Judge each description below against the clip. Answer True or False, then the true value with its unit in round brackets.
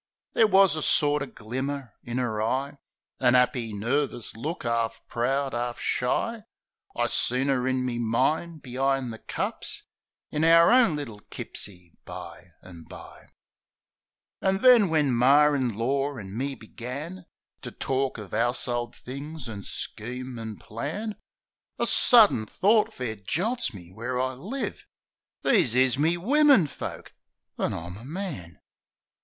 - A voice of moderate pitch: False (130 Hz)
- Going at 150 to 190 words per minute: False (140 wpm)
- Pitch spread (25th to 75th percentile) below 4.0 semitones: False (5.1 semitones)